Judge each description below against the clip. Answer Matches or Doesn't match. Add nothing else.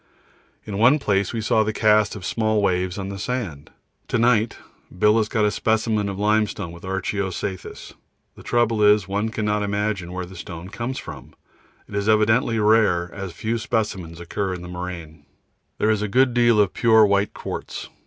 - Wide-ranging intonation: Doesn't match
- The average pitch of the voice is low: Matches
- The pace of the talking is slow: Doesn't match